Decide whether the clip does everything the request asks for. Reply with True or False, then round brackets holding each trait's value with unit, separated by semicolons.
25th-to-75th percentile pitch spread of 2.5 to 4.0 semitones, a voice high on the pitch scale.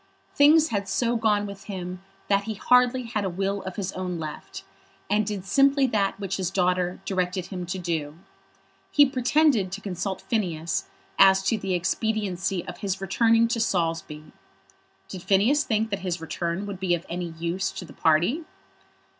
True (3.4 semitones; 195 Hz)